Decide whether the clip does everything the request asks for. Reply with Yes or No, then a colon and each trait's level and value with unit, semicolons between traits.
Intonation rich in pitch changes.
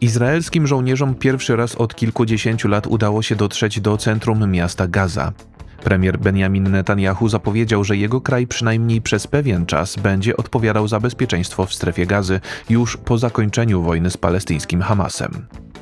No: average, 3.6 semitones